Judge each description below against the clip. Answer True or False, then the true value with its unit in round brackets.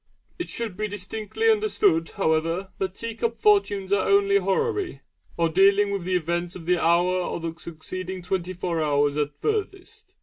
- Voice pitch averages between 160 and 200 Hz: True (190 Hz)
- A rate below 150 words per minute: False (170 wpm)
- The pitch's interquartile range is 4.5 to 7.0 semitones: True (5.0 semitones)